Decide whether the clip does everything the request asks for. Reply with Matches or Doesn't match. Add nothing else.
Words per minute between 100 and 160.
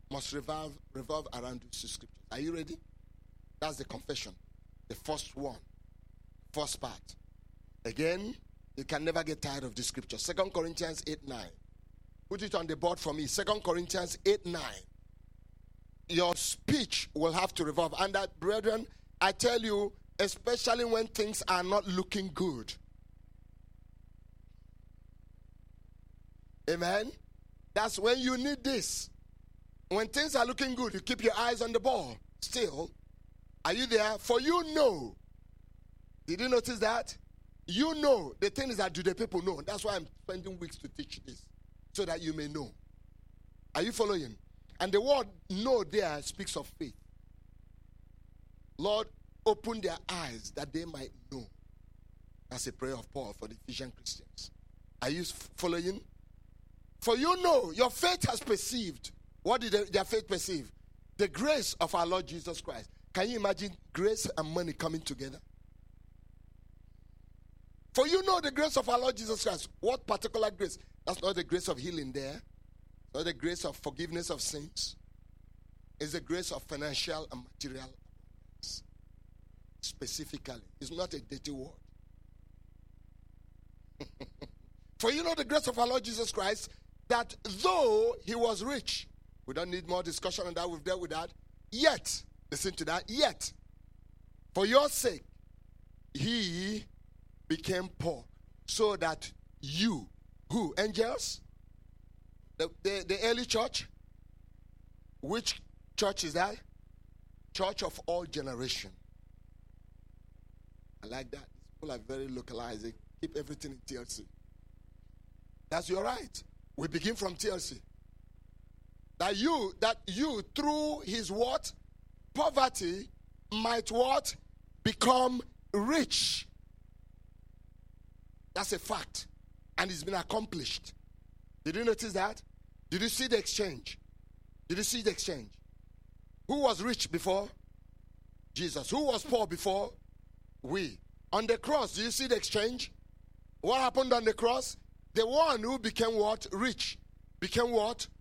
Matches